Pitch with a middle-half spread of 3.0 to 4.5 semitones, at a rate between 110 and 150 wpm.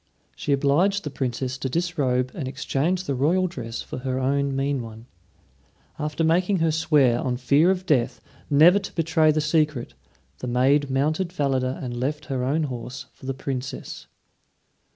No: average, 3.7 semitones; average, 165 wpm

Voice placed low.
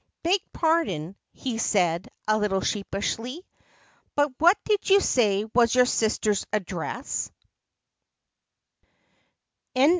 No: high, 225 Hz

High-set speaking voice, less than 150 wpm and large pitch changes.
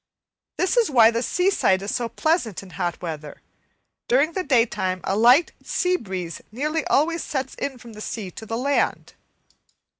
No: high, 240 Hz; average, 170 wpm; wide, 7.7 semitones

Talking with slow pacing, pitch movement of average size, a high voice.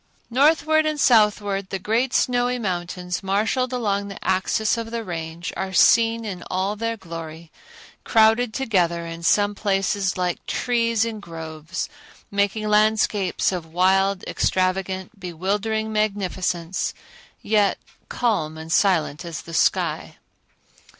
Yes: slow, 125 wpm; average, 3.7 semitones; high, 200 Hz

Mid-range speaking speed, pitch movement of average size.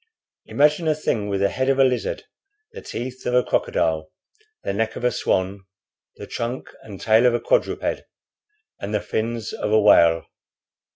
Yes: average, 175 wpm; average, 4.2 semitones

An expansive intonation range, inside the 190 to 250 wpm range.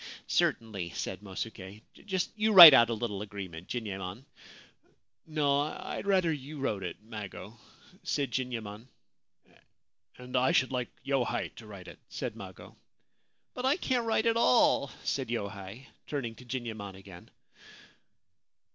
No: wide, 5.8 semitones; average, 155 wpm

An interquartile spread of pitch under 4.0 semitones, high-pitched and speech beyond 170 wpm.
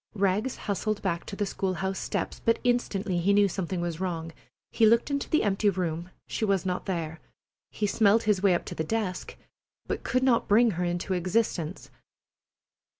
Yes: average, 3.4 semitones; high, 195 Hz; average, 185 wpm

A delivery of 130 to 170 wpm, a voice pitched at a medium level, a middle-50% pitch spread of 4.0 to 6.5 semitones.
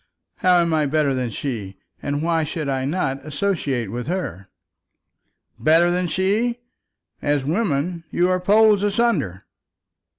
Yes: slow, 135 wpm; medium, 160 Hz; average, 5.2 semitones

